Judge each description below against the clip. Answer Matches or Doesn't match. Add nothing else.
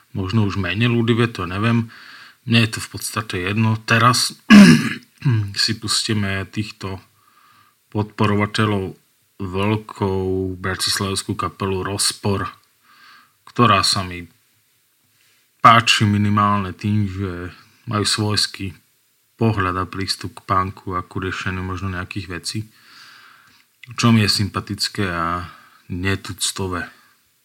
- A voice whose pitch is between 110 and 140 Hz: Doesn't match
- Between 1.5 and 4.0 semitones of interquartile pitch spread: Matches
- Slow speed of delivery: Matches